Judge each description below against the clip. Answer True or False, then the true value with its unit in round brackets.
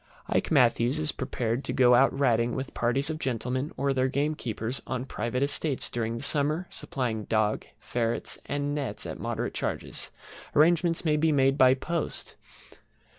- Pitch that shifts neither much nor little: True (3.4 semitones)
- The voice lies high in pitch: False (135 Hz)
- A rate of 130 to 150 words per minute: False (165 wpm)